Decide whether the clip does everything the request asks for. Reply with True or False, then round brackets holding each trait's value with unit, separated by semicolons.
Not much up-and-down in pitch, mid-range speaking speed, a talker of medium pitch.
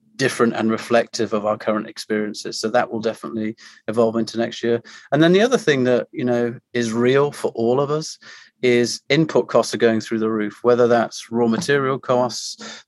False (1.7 semitones; 195 wpm; 115 Hz)